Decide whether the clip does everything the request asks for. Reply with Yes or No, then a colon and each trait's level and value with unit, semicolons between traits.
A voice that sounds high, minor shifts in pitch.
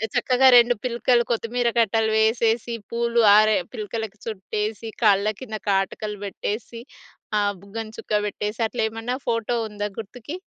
Yes: high, 225 Hz; narrow, 2.1 semitones